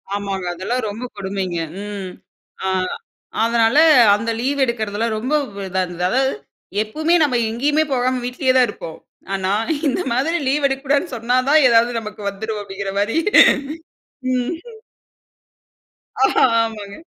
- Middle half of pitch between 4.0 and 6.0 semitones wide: Yes, average, 4.4 semitones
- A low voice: No, high, 230 Hz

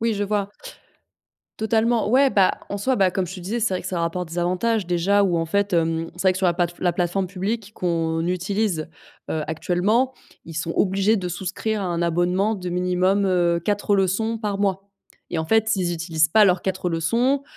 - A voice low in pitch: No, medium, 185 Hz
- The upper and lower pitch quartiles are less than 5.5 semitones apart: Yes, average, 2.9 semitones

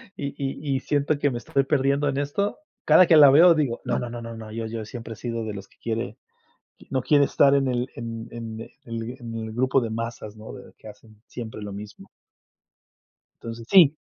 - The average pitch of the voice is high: No, low, 120 Hz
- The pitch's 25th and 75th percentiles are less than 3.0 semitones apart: No, average, 3.7 semitones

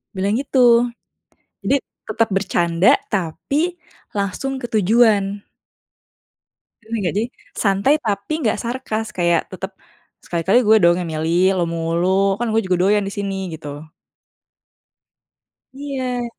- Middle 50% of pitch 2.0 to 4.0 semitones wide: No, average, 5.0 semitones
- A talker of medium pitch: No, high, 200 Hz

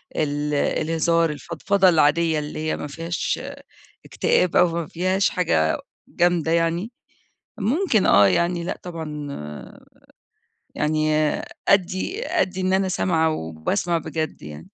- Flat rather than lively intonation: No, average, 3.2 semitones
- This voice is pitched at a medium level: Yes, medium, 165 Hz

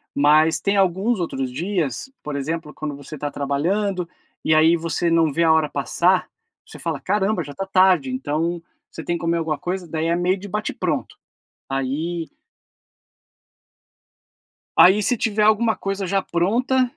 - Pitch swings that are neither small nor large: Yes, average, 4.3 semitones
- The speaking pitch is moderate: Yes, medium, 170 Hz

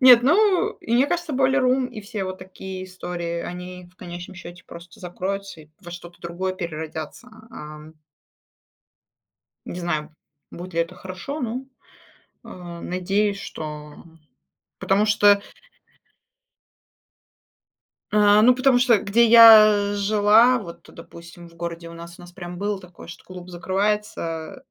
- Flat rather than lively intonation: No, average, 3.8 semitones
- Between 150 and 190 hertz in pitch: Yes, medium, 185 Hz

